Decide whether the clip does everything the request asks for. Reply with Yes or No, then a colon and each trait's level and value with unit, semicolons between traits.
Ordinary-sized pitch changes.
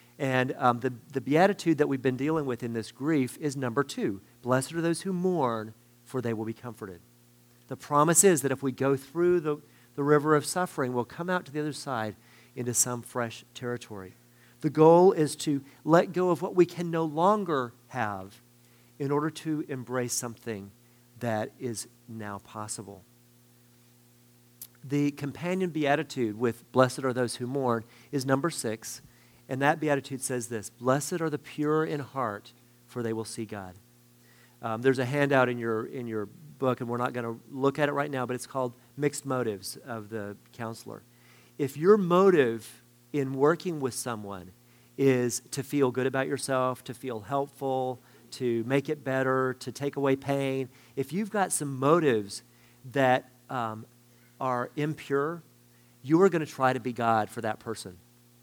Yes: average, 3.2 semitones